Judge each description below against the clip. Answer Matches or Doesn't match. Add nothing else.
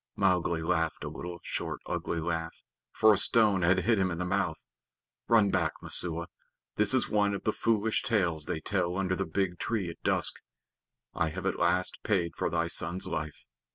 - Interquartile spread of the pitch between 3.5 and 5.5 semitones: Doesn't match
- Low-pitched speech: Matches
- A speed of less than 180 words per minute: Doesn't match